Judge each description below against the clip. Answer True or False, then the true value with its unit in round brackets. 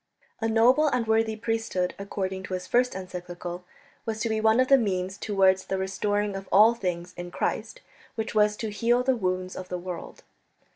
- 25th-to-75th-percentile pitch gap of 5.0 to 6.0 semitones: False (3.5 semitones)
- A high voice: True (205 Hz)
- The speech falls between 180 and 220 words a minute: True (190 wpm)